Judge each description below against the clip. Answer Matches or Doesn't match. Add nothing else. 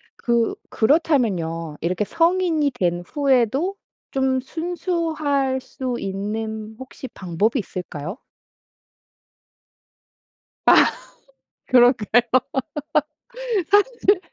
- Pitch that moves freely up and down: Matches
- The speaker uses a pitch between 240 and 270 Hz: Matches